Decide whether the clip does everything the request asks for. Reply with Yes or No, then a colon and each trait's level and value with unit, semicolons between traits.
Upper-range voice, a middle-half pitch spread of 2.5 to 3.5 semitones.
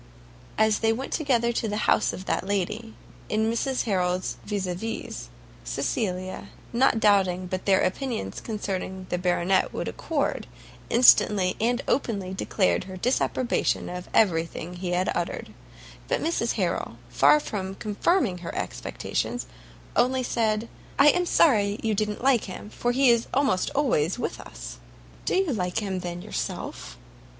No: high, 210 Hz; average, 4.5 semitones